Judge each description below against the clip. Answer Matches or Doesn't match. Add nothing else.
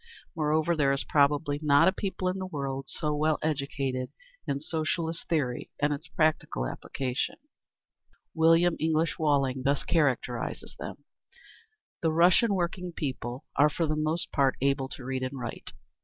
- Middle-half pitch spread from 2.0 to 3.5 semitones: Matches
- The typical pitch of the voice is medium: Matches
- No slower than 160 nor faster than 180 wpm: Doesn't match